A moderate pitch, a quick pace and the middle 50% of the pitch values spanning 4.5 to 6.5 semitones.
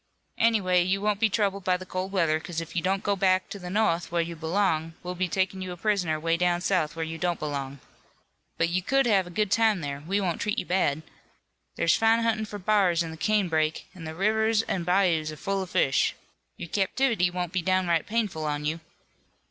No: medium, 180 Hz; fast, 220 wpm; average, 3.3 semitones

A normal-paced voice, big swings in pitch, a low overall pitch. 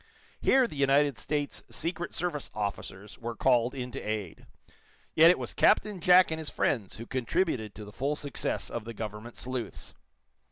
Yes: average, 170 wpm; wide, 6.3 semitones; low, 130 Hz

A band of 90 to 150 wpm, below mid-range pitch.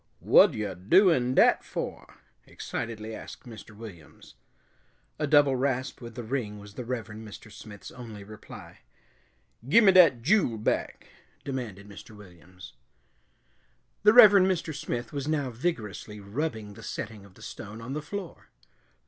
Yes: average, 140 wpm; low, 115 Hz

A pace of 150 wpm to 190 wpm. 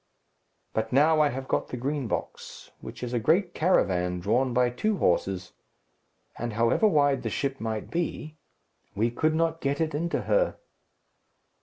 Yes: average, 160 wpm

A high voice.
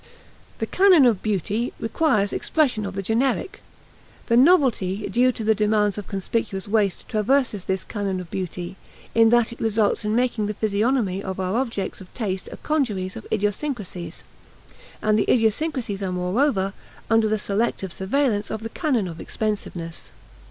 Yes: high, 215 Hz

